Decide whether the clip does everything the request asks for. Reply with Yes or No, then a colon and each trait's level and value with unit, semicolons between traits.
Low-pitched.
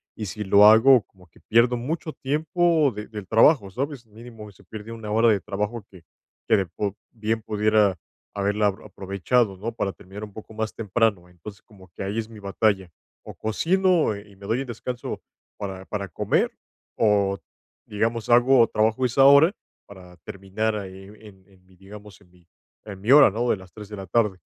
Yes: low, 105 Hz